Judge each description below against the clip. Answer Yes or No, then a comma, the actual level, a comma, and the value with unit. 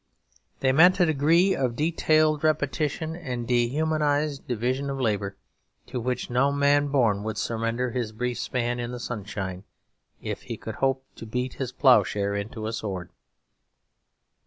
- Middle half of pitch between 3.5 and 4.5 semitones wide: Yes, average, 4.2 semitones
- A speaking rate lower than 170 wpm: Yes, average, 150 wpm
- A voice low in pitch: Yes, low, 125 Hz